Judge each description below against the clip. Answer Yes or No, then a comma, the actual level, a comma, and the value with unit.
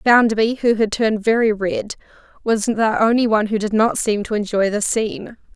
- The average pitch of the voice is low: No, high, 215 Hz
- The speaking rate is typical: Yes, average, 195 wpm